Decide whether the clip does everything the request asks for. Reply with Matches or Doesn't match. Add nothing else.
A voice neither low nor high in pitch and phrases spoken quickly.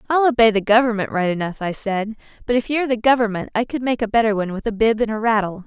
Doesn't match